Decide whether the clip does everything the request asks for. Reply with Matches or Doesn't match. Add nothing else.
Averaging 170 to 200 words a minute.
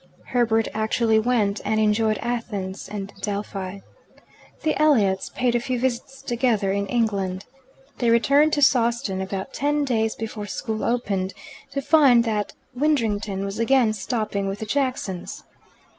Doesn't match